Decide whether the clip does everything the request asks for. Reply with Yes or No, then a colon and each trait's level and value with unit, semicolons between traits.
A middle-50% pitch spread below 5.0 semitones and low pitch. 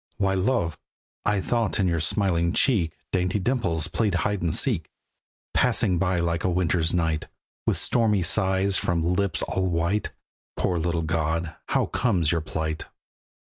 Yes: average, 3.1 semitones; very low, 90 Hz